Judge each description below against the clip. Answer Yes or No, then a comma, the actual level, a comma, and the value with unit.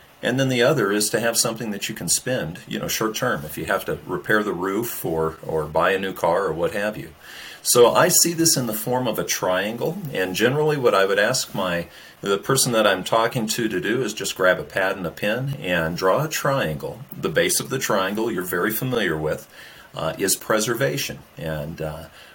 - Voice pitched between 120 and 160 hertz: No, low, 105 Hz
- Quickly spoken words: Yes, fast, 225 wpm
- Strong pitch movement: Yes, wide, 7.2 semitones